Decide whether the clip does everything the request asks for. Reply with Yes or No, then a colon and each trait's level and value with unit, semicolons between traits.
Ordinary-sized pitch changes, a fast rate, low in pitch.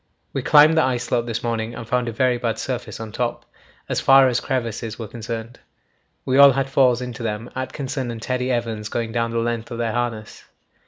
No: narrow, 2.0 semitones; fast, 210 wpm; low, 120 Hz